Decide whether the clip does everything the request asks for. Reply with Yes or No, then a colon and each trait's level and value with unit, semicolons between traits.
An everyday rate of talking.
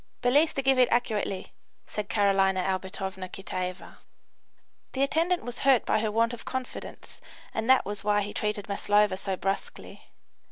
Yes: average, 155 wpm